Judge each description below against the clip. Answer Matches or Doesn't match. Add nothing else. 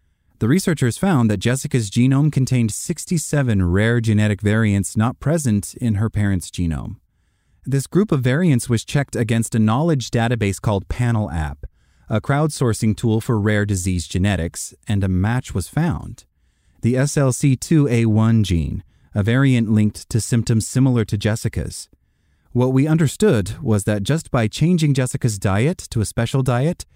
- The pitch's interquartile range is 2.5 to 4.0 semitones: Doesn't match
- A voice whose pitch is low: Matches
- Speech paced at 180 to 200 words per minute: Doesn't match